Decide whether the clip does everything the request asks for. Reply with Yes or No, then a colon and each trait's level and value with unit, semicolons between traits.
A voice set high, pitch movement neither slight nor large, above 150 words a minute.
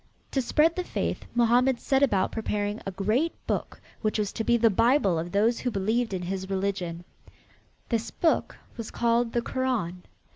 Yes: high, 225 Hz; average, 3.9 semitones; average, 175 wpm